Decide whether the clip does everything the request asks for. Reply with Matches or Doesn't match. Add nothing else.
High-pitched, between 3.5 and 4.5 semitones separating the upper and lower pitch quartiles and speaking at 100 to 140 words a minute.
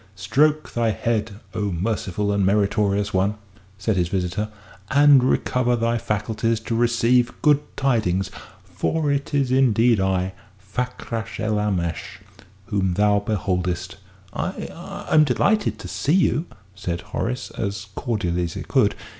Doesn't match